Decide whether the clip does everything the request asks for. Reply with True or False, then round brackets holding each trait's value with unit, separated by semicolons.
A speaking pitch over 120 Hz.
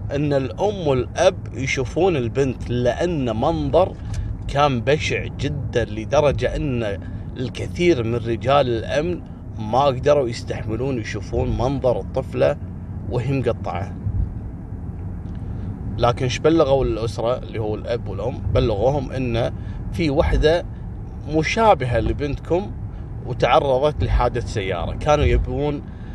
False (115 Hz)